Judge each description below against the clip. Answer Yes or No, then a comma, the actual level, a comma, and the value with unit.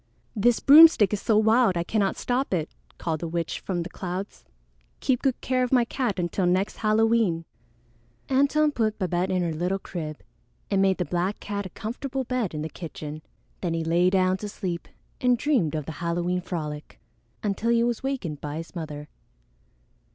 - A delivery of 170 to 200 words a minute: Yes, average, 180 wpm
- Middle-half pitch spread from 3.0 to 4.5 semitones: No, wide, 5.4 semitones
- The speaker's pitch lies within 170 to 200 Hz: Yes, high, 190 Hz